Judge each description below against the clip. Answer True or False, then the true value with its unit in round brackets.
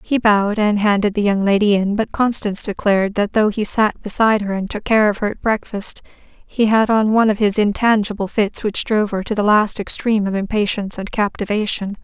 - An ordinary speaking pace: False (215 wpm)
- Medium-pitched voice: False (210 Hz)